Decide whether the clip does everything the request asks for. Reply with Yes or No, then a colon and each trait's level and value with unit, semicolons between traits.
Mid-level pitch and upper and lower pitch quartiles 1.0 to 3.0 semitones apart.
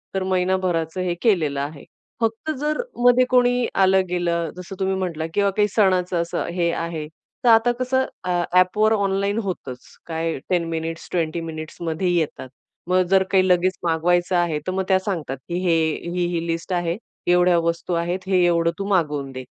Yes: medium, 180 Hz; narrow, 2.4 semitones